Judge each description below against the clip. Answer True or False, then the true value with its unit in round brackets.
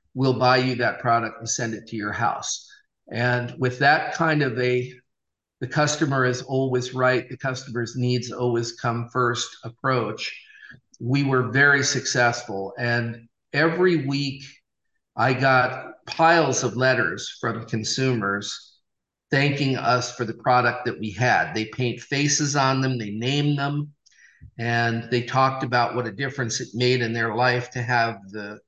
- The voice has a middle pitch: False (125 Hz)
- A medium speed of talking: True (155 wpm)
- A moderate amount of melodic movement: False (2.1 semitones)